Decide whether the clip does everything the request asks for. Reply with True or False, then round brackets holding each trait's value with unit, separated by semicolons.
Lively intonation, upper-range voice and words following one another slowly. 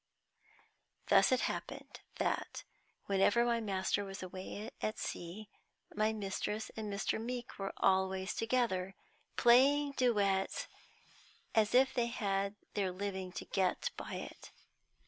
False (3.6 semitones; 205 Hz; 125 wpm)